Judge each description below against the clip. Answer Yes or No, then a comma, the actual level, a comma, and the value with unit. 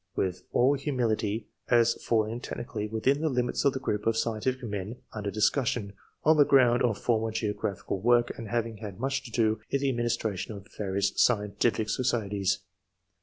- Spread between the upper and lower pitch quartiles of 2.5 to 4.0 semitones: Yes, average, 2.9 semitones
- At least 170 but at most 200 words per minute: Yes, average, 175 wpm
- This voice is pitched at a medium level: No, low, 115 Hz